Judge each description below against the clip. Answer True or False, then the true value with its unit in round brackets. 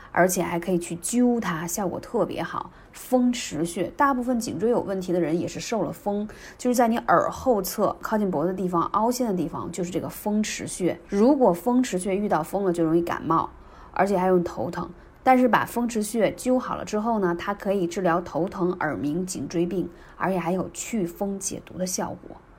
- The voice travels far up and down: False (4.9 semitones)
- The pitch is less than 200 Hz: True (190 Hz)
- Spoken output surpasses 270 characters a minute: True (300 characters per minute)